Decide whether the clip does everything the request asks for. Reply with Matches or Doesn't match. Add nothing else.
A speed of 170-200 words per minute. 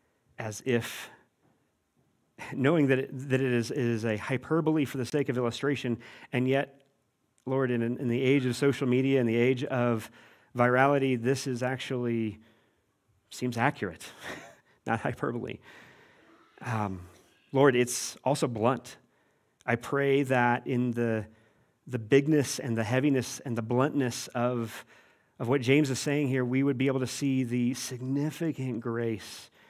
Doesn't match